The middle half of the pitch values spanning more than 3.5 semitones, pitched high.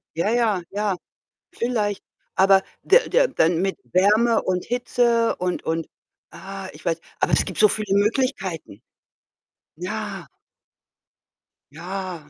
Yes: average, 4.0 semitones; high, 195 Hz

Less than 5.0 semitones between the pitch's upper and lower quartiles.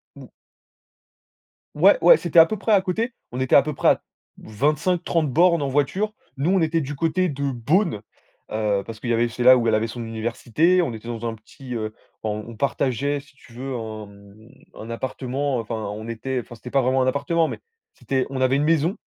No: wide, 5.4 semitones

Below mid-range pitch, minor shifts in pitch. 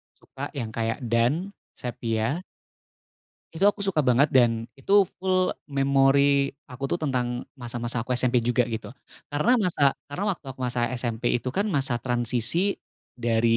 No: low, 125 Hz; average, 3.3 semitones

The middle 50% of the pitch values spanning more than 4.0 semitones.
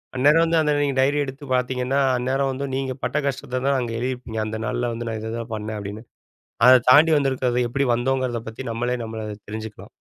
No: average, 3.0 semitones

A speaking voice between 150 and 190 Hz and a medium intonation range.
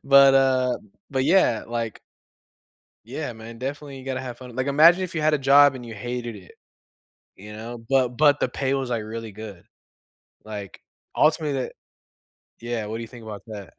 No: low, 125 Hz; average, 3.5 semitones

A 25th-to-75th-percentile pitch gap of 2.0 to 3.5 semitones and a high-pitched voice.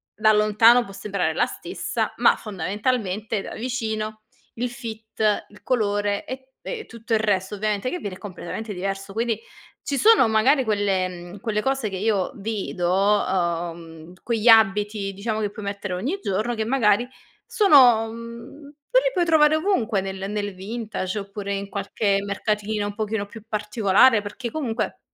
Yes: average, 2.7 semitones; high, 215 Hz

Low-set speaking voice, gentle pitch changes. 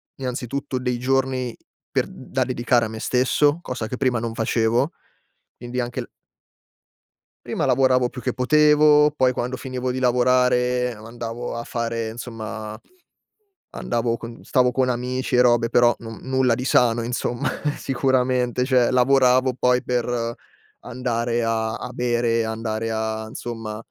Yes: low, 125 Hz; narrow, 1.6 semitones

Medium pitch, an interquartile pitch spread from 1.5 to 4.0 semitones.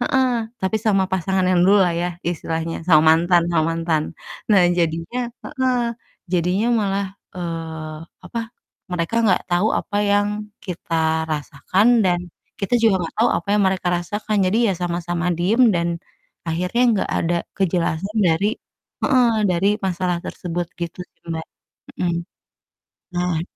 Yes: medium, 180 Hz; average, 3.1 semitones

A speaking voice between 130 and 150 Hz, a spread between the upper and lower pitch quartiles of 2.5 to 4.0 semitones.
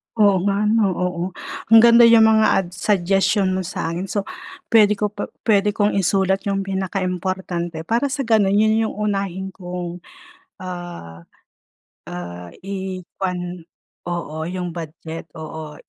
No: high, 190 Hz; average, 2.8 semitones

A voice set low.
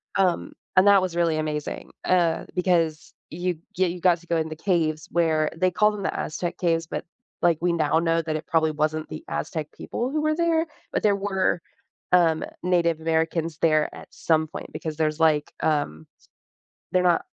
No: medium, 165 Hz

